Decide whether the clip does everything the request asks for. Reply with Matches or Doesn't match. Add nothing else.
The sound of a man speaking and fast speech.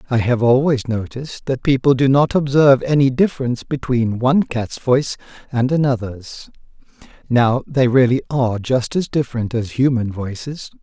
Doesn't match